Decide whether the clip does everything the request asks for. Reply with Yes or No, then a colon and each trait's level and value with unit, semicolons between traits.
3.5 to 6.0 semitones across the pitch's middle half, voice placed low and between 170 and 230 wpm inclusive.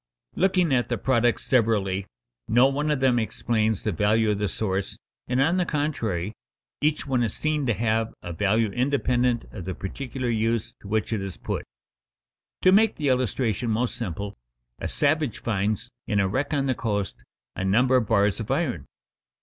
Yes: average, 4.4 semitones; low, 115 Hz; average, 180 wpm